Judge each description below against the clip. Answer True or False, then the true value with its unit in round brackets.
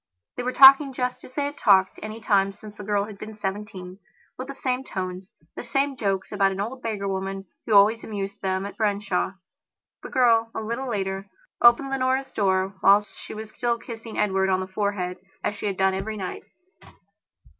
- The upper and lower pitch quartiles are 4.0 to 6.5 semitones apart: False (3.5 semitones)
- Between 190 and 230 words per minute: True (195 wpm)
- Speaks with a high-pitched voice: True (210 Hz)